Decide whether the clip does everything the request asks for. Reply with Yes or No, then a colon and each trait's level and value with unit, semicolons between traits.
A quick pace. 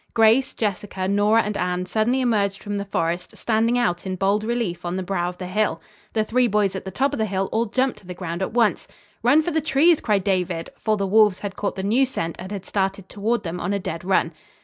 Yes: fast, 245 wpm